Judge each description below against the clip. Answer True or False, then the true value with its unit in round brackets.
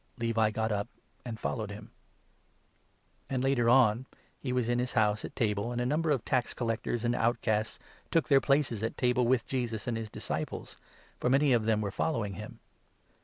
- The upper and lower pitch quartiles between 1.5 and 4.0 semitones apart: True (2.5 semitones)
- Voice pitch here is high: False (120 Hz)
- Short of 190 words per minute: False (195 wpm)